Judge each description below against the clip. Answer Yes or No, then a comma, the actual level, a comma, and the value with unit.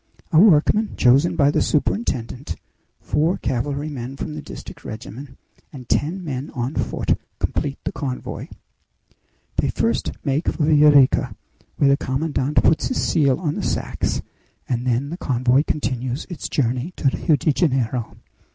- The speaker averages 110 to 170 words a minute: Yes, average, 150 wpm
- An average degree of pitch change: Yes, average, 3.1 semitones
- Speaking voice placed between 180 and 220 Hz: No, medium, 140 Hz